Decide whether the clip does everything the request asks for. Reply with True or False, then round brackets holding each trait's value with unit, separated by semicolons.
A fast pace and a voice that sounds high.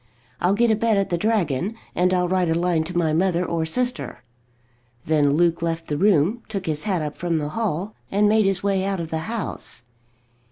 False (210 wpm; 180 Hz)